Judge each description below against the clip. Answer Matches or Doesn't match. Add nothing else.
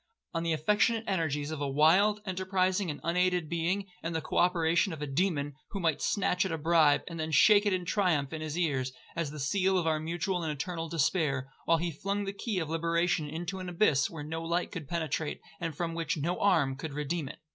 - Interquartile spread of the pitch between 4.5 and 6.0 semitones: Doesn't match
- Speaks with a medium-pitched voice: Matches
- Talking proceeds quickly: Matches